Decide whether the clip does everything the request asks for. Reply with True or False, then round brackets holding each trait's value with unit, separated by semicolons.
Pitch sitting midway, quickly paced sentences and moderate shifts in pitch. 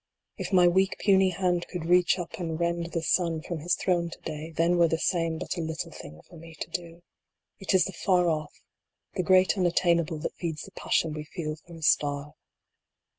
False (170 Hz; 225 wpm; 1.8 semitones)